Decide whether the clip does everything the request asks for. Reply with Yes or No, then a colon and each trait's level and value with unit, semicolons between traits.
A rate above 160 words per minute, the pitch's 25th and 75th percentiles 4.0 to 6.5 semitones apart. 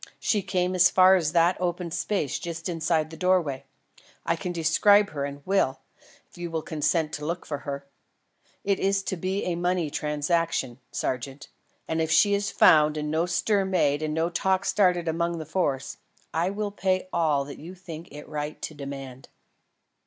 No: average, 180 wpm; average, 3.5 semitones